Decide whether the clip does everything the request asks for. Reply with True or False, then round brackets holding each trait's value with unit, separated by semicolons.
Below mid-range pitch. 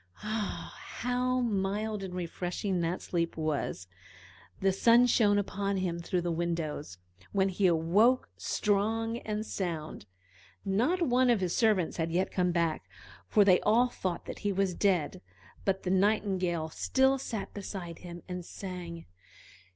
False (190 Hz)